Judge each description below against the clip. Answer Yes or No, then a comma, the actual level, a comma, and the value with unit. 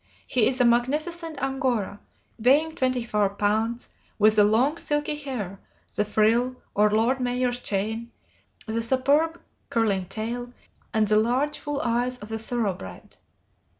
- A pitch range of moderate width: Yes, average, 3.6 semitones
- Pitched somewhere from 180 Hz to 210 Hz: No, high, 235 Hz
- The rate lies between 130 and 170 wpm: Yes, average, 140 wpm